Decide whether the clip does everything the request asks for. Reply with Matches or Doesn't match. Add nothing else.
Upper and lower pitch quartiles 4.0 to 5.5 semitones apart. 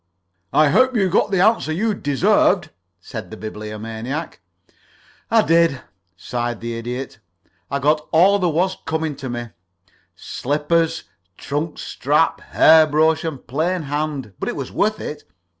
Matches